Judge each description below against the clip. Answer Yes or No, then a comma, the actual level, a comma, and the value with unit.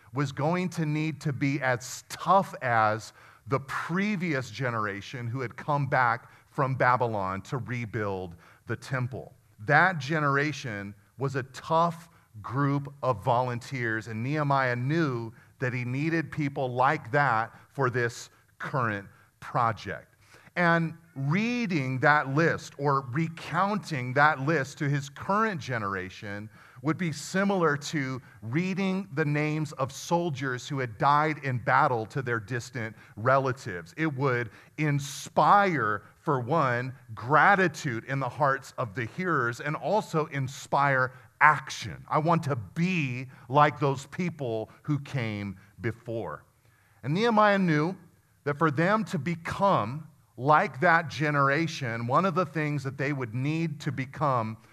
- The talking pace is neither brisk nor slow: No, slow, 130 wpm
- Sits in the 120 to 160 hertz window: Yes, medium, 140 Hz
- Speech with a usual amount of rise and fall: Yes, average, 4.6 semitones